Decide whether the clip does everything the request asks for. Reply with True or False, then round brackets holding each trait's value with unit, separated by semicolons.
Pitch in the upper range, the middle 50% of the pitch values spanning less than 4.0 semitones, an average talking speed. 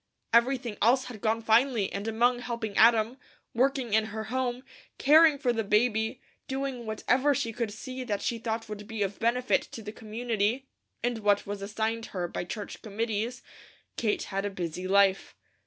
True (225 Hz; 2.8 semitones; 170 wpm)